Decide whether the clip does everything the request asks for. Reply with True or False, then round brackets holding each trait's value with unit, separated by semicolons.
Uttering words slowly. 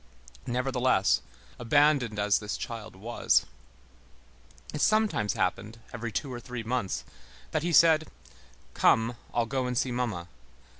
True (130 wpm)